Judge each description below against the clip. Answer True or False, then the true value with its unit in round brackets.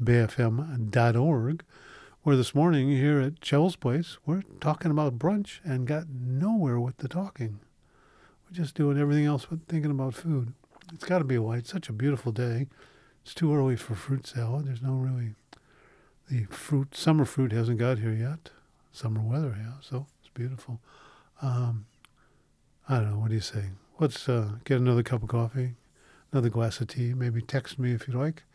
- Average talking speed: True (180 wpm)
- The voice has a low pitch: True (130 Hz)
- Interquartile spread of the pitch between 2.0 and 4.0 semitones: True (3.7 semitones)